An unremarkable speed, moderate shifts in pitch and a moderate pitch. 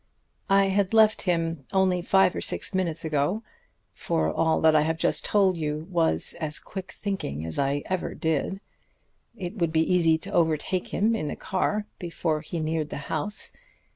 Yes: average, 175 wpm; average, 3.6 semitones; medium, 165 Hz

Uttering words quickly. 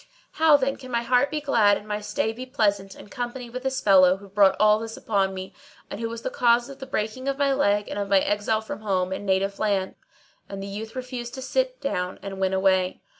Yes: fast, 240 wpm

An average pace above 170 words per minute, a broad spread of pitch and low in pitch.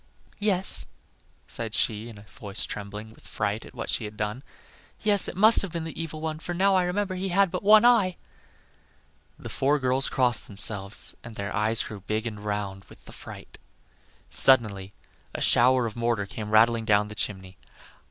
Yes: average, 185 wpm; wide, 8.2 semitones; low, 115 Hz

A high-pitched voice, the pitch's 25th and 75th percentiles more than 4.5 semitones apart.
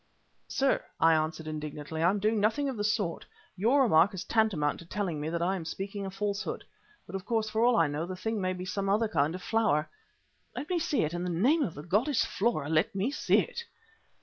Yes: high, 195 Hz; average, 5.2 semitones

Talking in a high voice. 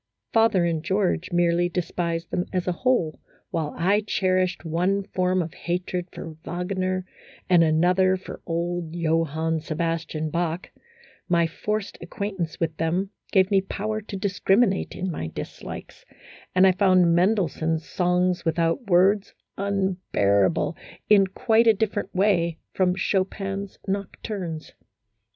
No: medium, 180 Hz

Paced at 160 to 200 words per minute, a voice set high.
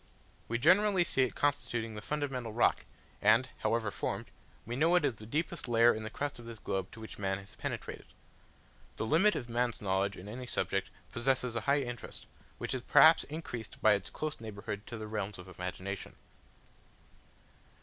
No: average, 180 wpm; low, 115 Hz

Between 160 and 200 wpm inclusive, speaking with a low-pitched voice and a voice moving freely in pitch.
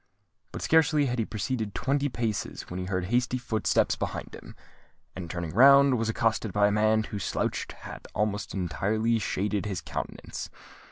No: average, 165 wpm; low, 110 Hz; average, 3.8 semitones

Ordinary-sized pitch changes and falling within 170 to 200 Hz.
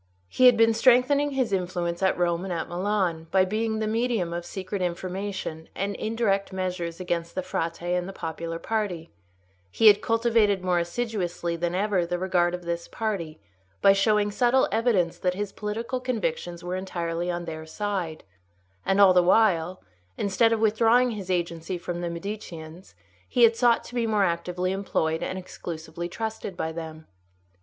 Yes: average, 3.9 semitones; medium, 185 Hz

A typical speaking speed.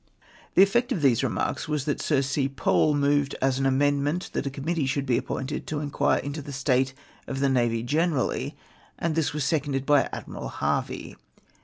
Yes: average, 190 wpm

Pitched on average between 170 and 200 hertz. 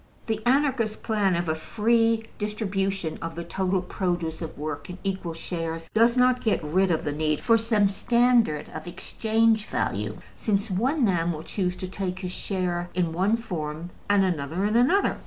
Yes: high, 190 Hz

